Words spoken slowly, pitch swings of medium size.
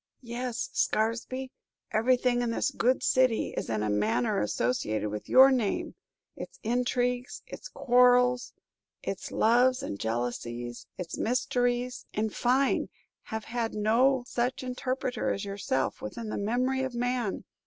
Yes: slow, 130 wpm; average, 3.8 semitones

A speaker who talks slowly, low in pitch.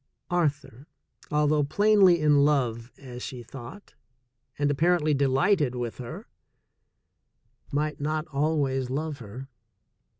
No: slow, 105 wpm; medium, 145 Hz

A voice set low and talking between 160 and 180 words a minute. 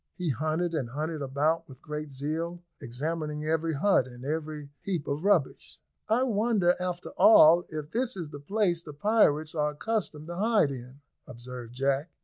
No: medium, 155 Hz; average, 165 wpm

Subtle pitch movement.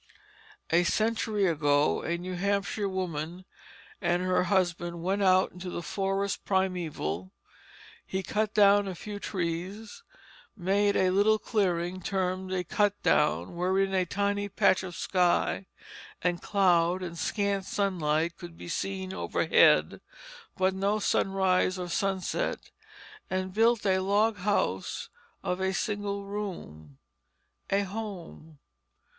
Yes: narrow, 2.3 semitones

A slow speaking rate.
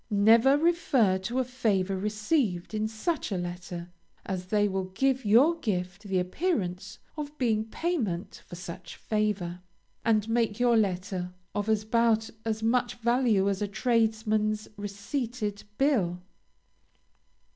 Yes: slow, 130 wpm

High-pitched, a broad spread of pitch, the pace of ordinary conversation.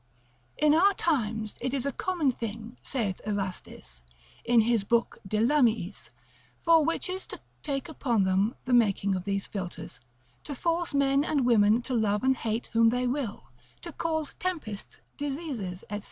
Yes: high, 240 Hz; wide, 5.7 semitones; average, 160 wpm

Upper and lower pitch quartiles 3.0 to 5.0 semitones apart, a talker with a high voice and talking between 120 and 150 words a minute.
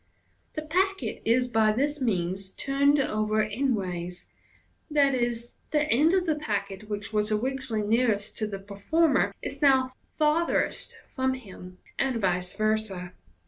No: wide, 5.4 semitones; high, 225 Hz; average, 140 wpm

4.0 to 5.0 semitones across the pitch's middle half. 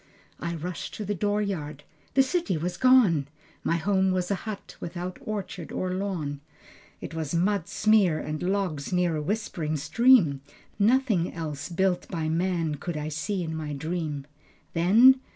Yes: average, 4.4 semitones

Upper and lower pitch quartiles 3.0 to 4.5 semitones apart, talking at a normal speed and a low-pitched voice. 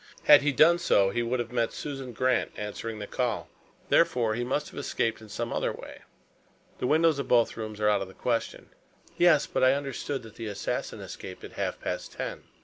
No: average, 4.1 semitones; fast, 210 wpm; low, 120 Hz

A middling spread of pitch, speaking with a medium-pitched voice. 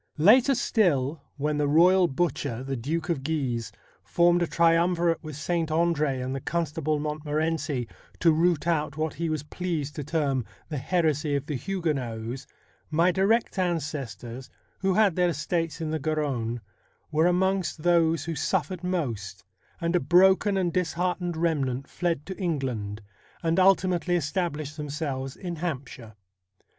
Yes: average, 3.8 semitones; medium, 160 Hz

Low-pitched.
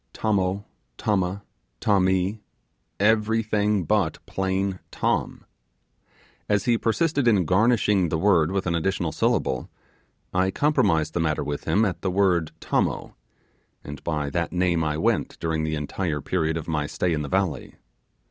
Yes: very low, 95 Hz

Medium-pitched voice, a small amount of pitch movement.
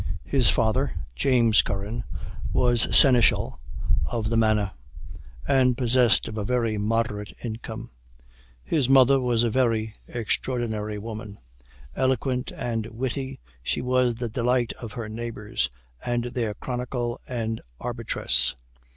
No: low, 120 Hz; narrow, 2.2 semitones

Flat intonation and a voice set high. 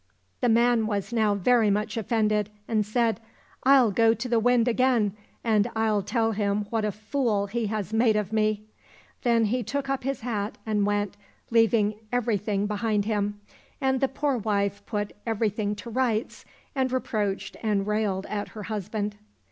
Yes: narrow, 2.3 semitones; high, 215 Hz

